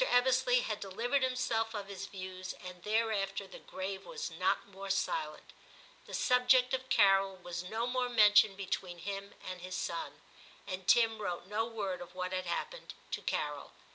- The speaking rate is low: No, average, 170 wpm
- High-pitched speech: Yes, high, 200 Hz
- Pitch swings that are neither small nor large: Yes, average, 4.5 semitones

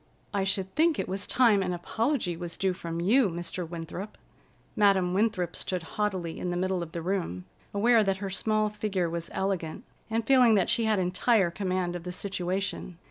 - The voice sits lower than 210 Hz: Yes, high, 190 Hz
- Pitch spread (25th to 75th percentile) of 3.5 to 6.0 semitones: No, average, 3.1 semitones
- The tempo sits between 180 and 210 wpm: Yes, average, 190 wpm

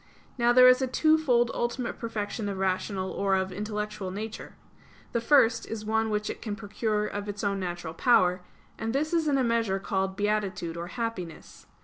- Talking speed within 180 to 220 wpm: Yes, average, 185 wpm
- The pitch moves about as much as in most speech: Yes, average, 3.5 semitones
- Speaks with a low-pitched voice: No, high, 210 Hz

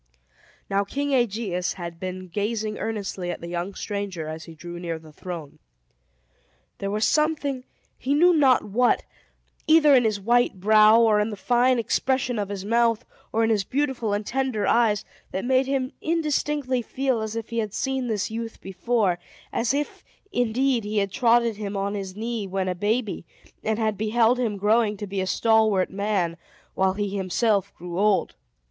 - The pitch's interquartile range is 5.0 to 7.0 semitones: No, average, 3.8 semitones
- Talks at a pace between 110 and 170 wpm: No, average, 180 wpm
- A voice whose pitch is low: No, high, 215 Hz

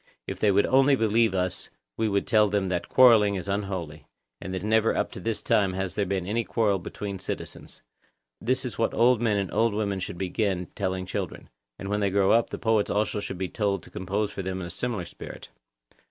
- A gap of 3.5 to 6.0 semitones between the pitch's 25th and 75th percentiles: No, average, 2.9 semitones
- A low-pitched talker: Yes, low, 100 Hz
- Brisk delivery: Yes, fast, 225 wpm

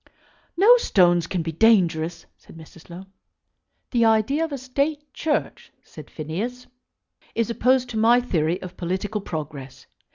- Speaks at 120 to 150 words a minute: Yes, average, 140 wpm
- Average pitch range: No, wide, 6.9 semitones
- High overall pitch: Yes, high, 210 Hz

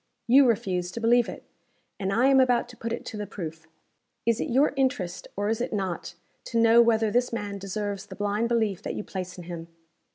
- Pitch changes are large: No, average, 3.5 semitones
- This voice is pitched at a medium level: No, high, 215 Hz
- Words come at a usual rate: No, fast, 220 wpm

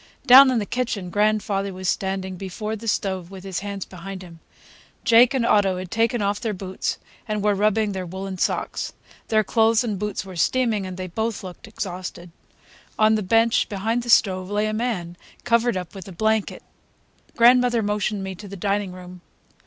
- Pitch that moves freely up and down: No, average, 2.9 semitones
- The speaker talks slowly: No, average, 185 wpm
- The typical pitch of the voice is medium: No, high, 205 Hz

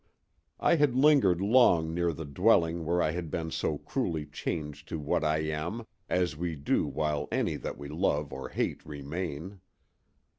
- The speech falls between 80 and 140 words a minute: No, average, 170 wpm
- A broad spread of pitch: No, average, 3.1 semitones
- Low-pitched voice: Yes, very low, 80 Hz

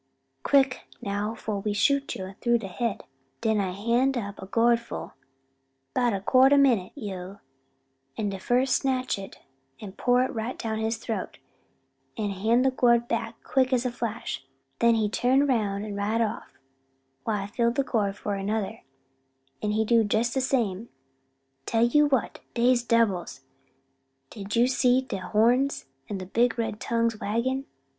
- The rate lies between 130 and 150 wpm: No, average, 165 wpm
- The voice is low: No, high, 230 Hz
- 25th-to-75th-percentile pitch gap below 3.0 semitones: No, average, 3.3 semitones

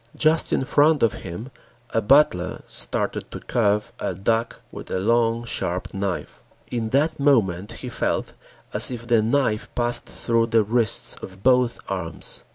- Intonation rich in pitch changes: No, average, 3.9 semitones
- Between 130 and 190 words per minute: Yes, average, 160 wpm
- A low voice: Yes, low, 115 Hz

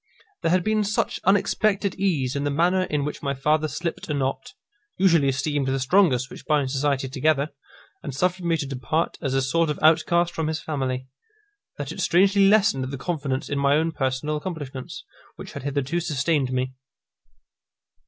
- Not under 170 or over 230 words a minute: Yes, average, 175 wpm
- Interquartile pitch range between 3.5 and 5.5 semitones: Yes, average, 4.2 semitones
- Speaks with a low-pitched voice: No, medium, 150 Hz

